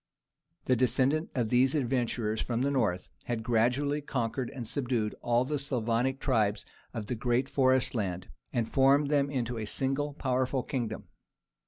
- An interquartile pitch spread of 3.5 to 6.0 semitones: No, average, 2.9 semitones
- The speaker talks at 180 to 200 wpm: No, average, 155 wpm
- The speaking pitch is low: Yes, low, 125 Hz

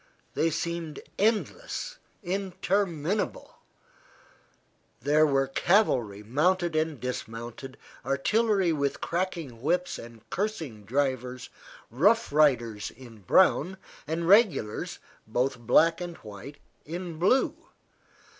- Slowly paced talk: Yes, slow, 95 wpm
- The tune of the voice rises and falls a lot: Yes, wide, 6.4 semitones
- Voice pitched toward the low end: No, medium, 155 Hz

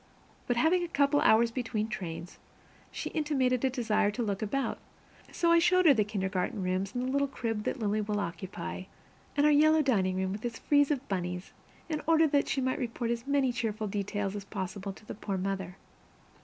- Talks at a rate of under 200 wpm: No, fast, 205 wpm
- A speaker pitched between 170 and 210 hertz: No, high, 225 Hz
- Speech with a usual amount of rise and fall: No, wide, 5.9 semitones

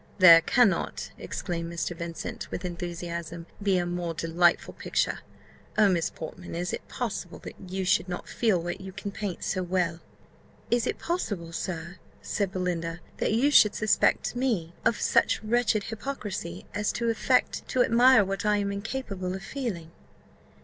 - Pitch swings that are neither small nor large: Yes, average, 3.8 semitones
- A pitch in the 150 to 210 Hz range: Yes, medium, 185 Hz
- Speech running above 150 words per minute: Yes, average, 160 wpm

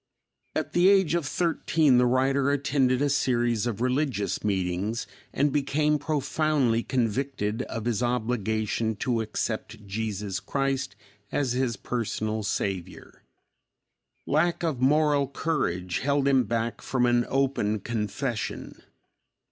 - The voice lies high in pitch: No, low, 125 Hz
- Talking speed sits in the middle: No, slow, 120 wpm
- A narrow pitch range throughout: No, average, 4.3 semitones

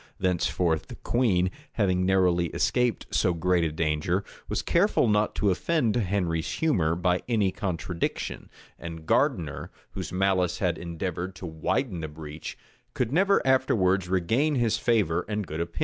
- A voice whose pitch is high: No, very low, 95 Hz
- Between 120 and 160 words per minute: Yes, average, 150 wpm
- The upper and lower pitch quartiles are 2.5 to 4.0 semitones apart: No, average, 4.8 semitones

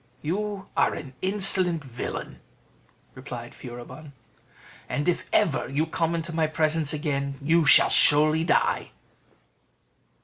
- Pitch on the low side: No, medium, 155 Hz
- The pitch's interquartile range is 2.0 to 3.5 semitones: Yes, average, 3.1 semitones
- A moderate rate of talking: No, slow, 115 wpm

